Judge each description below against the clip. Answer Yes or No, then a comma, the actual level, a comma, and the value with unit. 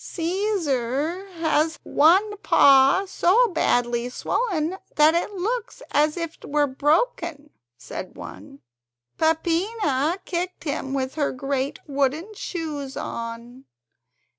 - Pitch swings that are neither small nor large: Yes, average, 5.0 semitones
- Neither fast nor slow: No, slow, 110 wpm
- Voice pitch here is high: Yes, very high, 310 Hz